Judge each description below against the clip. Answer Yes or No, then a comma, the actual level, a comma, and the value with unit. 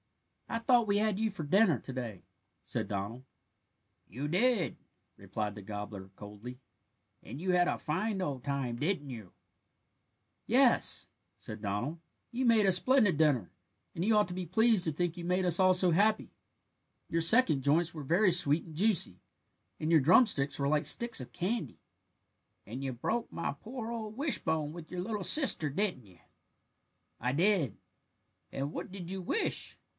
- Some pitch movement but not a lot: No, wide, 7.3 semitones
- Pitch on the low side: No, medium, 170 Hz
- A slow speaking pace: No, average, 170 wpm